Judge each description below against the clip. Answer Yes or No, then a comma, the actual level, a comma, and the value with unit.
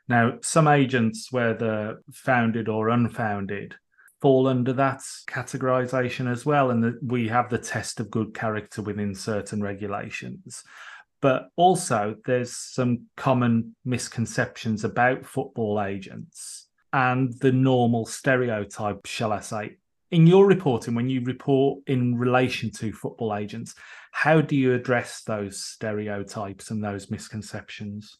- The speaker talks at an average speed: No, slow, 130 wpm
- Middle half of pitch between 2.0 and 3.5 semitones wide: Yes, average, 3.1 semitones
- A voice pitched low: Yes, low, 120 Hz